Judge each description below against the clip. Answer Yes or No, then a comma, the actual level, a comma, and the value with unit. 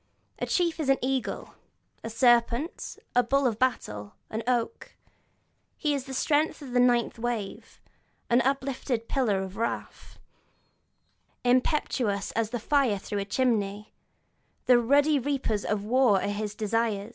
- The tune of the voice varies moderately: Yes, average, 4.0 semitones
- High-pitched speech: Yes, high, 240 Hz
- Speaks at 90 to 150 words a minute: Yes, average, 145 wpm